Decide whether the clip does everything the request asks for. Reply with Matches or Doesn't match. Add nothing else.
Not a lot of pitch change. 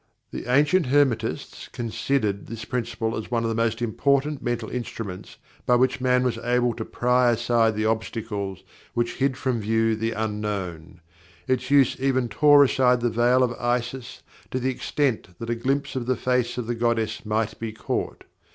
Matches